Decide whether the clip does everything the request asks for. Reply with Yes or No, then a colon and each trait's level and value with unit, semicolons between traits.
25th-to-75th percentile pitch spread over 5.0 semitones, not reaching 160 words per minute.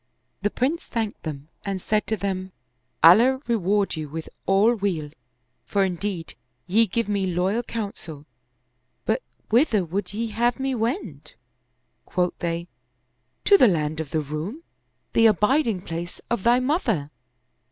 Yes: wide, 5.4 semitones; average, 150 wpm